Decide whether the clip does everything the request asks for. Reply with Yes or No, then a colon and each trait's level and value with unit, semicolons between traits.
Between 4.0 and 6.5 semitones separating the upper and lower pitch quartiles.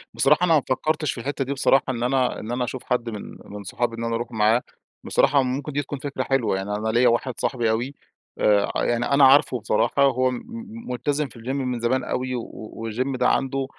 No: average, 2.8 semitones